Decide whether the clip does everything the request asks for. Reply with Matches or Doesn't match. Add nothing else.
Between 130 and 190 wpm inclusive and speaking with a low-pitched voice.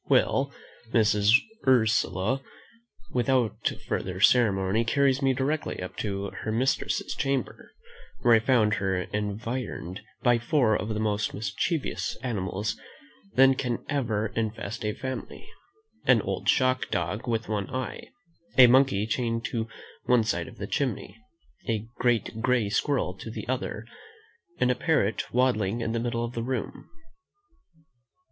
Matches